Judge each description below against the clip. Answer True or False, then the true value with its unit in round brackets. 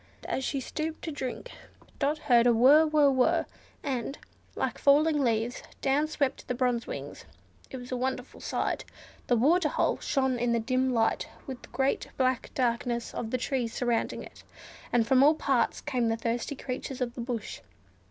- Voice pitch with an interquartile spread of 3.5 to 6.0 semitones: False (2.7 semitones)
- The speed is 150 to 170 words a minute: False (180 wpm)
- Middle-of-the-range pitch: False (255 Hz)